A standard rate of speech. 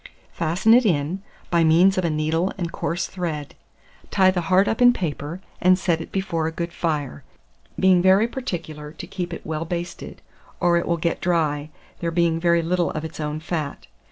Yes: average, 190 wpm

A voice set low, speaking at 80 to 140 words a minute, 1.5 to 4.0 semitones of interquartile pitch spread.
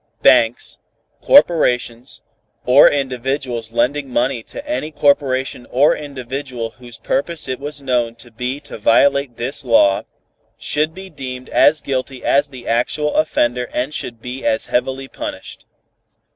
Yes: low, 130 Hz; slow, 135 wpm; average, 2.9 semitones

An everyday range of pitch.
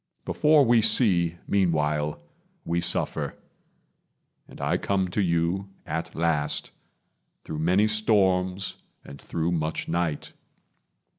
Yes: average, 3.3 semitones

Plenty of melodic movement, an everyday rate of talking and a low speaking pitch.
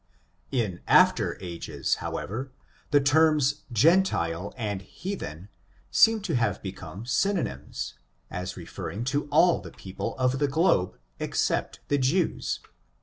No: wide, 8.3 semitones; slow, 125 wpm; low, 130 Hz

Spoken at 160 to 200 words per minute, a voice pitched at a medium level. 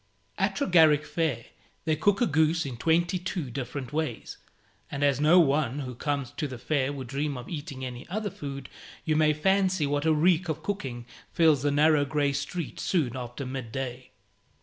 Yes: average, 185 wpm; medium, 145 Hz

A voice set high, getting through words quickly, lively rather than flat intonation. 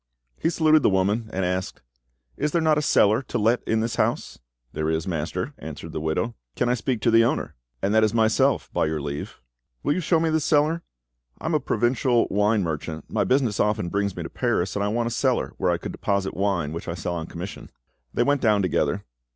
No: low, 105 Hz; fast, 225 wpm; wide, 5.7 semitones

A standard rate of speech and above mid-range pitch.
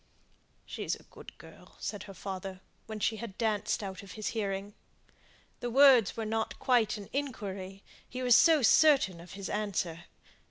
Yes: average, 160 wpm; high, 210 Hz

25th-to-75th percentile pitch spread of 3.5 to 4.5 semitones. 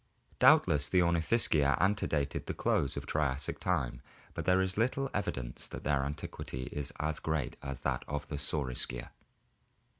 Yes: average, 3.9 semitones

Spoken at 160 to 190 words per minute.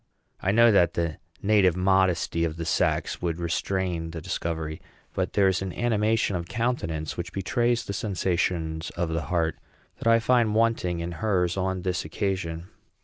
Yes: average, 165 wpm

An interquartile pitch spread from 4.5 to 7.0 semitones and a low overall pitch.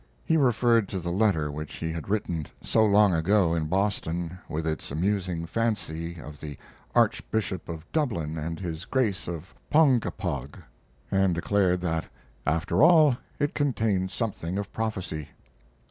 Yes: average, 4.9 semitones; very low, 90 Hz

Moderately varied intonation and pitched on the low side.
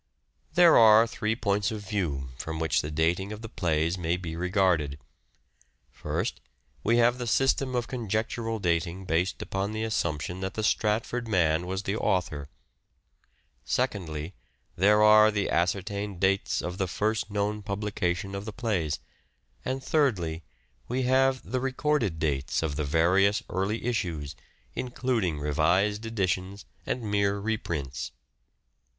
Yes: average, 4.6 semitones; low, 100 Hz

